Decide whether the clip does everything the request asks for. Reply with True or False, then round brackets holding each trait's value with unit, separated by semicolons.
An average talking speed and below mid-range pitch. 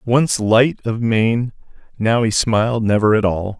True (165 wpm; 115 Hz)